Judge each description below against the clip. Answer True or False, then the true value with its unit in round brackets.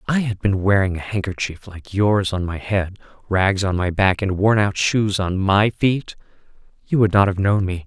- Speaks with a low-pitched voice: True (100 Hz)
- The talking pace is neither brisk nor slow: False (220 wpm)